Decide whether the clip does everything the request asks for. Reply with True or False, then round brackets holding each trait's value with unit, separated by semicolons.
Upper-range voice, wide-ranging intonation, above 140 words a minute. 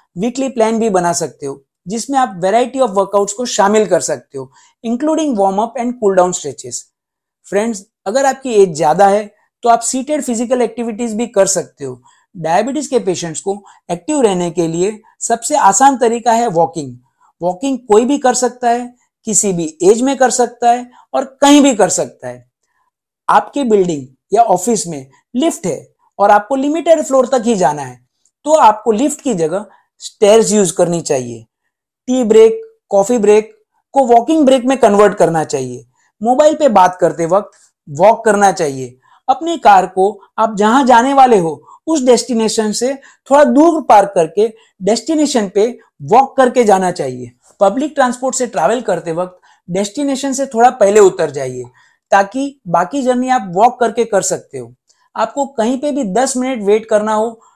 True (225 Hz; 6.1 semitones; 160 wpm)